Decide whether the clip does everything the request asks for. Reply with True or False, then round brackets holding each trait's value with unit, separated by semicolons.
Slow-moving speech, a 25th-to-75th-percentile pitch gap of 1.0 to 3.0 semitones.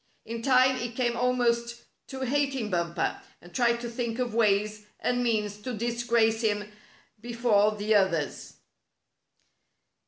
True (130 wpm; 2.5 semitones)